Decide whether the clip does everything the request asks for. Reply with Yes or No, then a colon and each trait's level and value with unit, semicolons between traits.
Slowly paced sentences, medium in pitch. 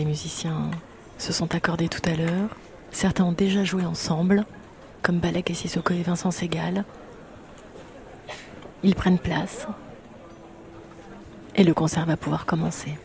Yes: slow, 135 wpm; medium, 175 Hz